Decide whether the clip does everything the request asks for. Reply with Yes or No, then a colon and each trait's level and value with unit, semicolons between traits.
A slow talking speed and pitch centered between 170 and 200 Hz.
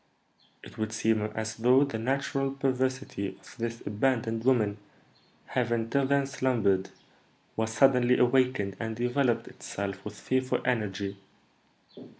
No: slow, 125 wpm; low, 120 Hz